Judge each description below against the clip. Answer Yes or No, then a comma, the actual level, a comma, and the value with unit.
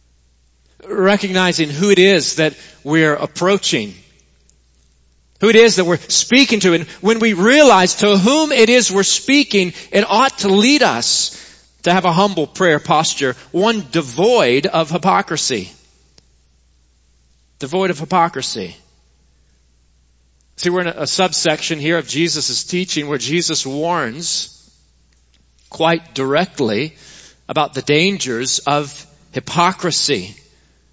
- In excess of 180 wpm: No, slow, 120 wpm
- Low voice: No, medium, 160 Hz